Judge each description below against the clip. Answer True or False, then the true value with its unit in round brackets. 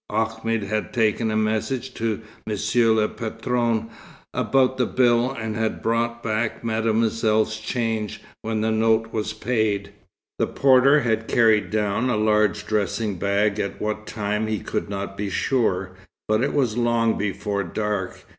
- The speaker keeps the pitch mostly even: True (1.5 semitones)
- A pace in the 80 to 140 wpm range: False (150 wpm)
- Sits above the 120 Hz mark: False (110 Hz)